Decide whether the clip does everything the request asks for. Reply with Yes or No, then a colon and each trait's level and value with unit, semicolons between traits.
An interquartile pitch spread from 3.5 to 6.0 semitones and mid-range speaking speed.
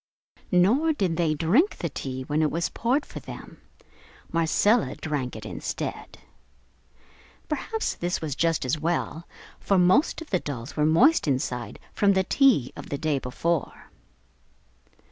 Yes: wide, 5.6 semitones; average, 145 wpm